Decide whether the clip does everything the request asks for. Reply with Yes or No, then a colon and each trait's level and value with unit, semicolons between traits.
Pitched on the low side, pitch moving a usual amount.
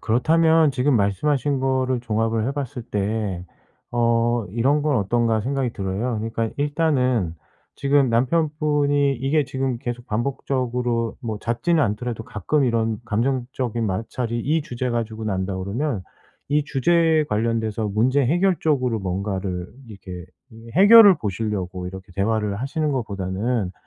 Yes: low, 120 Hz; average, 4.6 semitones